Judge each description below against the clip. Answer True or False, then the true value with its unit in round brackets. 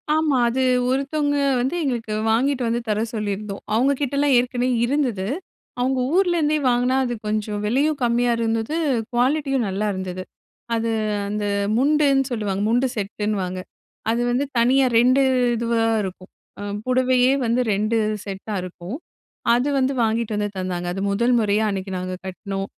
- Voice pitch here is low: False (235 Hz)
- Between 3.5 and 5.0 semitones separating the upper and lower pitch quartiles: True (4.2 semitones)